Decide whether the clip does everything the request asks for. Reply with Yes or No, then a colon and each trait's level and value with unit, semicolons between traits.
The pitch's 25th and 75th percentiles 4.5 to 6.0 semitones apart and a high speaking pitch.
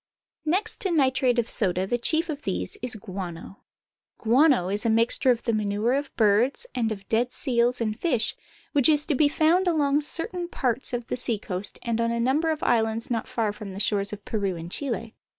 Yes: average, 5.0 semitones; high, 235 Hz